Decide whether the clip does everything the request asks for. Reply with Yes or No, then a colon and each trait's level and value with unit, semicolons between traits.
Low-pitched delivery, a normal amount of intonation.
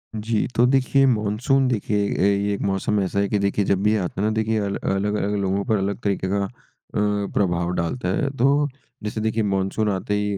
No: low, 105 Hz; narrow, 2.0 semitones